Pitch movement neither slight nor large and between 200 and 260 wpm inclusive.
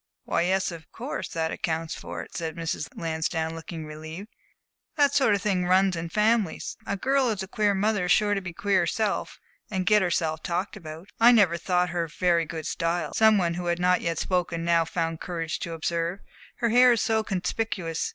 Yes: average, 3.7 semitones; fast, 205 wpm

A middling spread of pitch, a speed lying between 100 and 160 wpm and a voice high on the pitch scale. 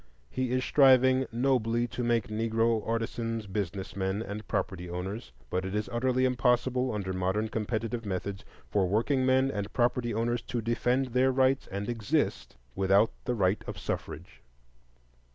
No: average, 3.8 semitones; average, 150 wpm; low, 115 Hz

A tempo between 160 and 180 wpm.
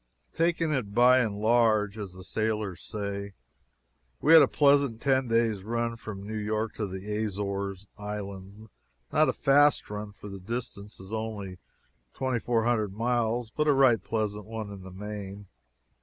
Yes: average, 165 wpm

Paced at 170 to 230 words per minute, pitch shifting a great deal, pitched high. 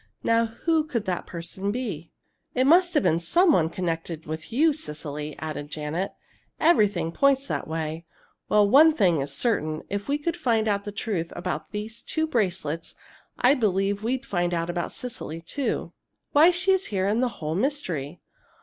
Yes: average, 175 wpm; wide, 8.1 semitones; high, 200 Hz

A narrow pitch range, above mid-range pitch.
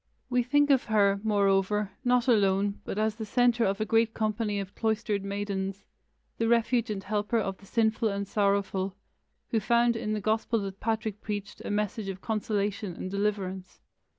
Yes: narrow, 2.1 semitones; high, 210 Hz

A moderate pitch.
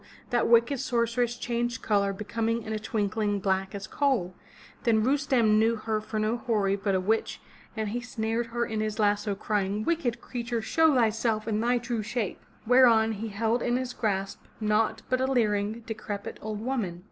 No: high, 220 Hz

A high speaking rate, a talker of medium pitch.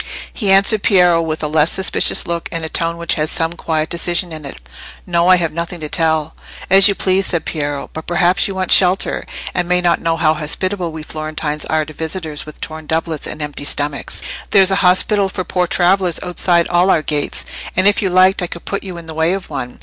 Yes: fast, 225 wpm; medium, 170 Hz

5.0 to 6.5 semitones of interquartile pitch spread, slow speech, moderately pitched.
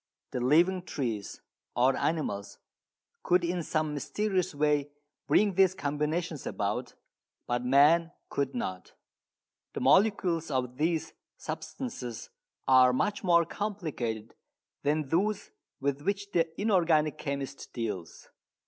Yes: wide, 5.5 semitones; slow, 110 wpm; medium, 150 Hz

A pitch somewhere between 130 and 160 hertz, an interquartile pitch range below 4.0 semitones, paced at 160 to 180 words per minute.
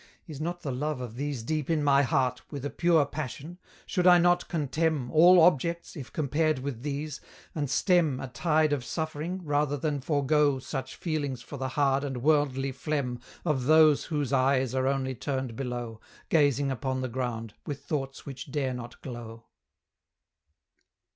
Yes: medium, 140 Hz; average, 2.9 semitones; average, 165 wpm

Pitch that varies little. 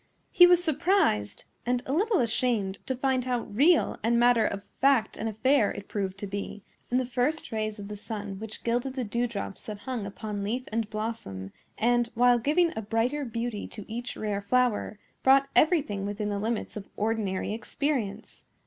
No: average, 3.7 semitones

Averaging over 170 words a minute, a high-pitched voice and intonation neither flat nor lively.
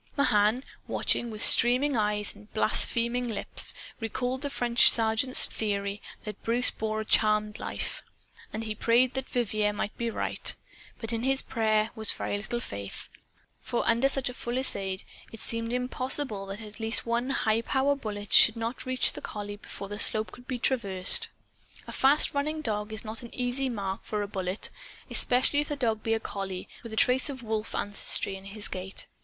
Yes: average, 180 wpm; high, 225 Hz; average, 3.0 semitones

